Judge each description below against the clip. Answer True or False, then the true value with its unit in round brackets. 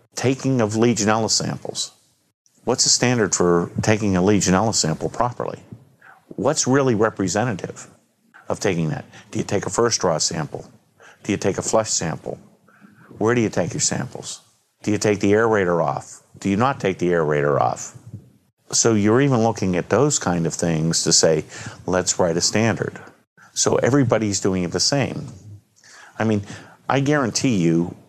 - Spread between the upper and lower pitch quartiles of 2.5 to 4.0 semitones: False (5.0 semitones)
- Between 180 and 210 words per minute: False (165 wpm)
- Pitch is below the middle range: True (105 Hz)